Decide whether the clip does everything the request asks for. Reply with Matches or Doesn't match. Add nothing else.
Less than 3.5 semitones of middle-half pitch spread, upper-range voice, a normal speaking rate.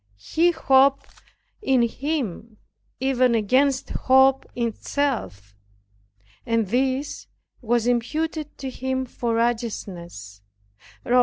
Doesn't match